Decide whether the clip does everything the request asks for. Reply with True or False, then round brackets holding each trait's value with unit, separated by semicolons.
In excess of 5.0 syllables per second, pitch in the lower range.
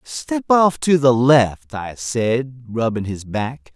False (3.1 syllables/s; 125 Hz)